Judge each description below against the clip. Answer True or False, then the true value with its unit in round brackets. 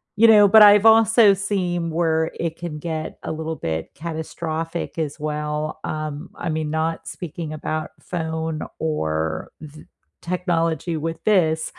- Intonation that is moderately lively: False (2.1 semitones)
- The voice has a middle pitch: True (160 Hz)